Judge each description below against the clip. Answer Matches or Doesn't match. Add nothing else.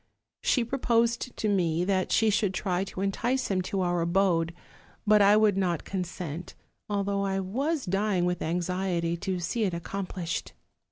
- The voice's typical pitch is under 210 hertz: Matches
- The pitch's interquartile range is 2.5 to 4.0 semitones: Matches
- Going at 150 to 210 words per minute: Matches